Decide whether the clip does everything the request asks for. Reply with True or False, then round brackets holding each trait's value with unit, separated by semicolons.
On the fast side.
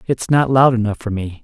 True (250 wpm)